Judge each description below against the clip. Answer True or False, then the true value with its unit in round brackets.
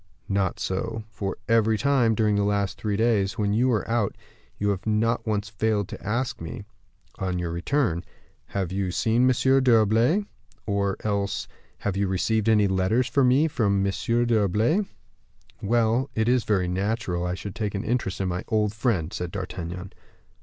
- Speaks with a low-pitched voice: True (105 Hz)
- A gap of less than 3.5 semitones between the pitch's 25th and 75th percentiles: True (3.1 semitones)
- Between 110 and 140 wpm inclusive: False (175 wpm)